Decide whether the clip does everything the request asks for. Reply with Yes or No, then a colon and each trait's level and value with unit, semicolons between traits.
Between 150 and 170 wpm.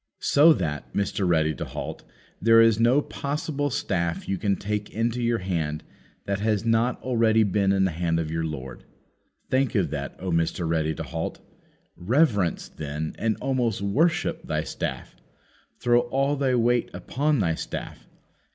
Yes: average, 160 wpm